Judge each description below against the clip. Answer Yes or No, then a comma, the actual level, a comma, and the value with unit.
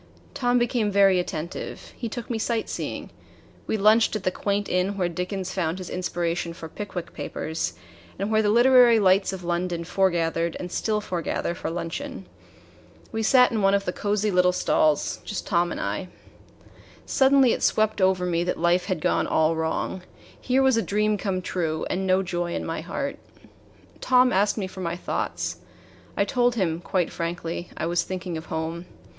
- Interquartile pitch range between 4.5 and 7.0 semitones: No, average, 3.8 semitones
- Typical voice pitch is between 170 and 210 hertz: Yes, medium, 185 Hz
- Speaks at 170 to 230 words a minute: Yes, average, 180 wpm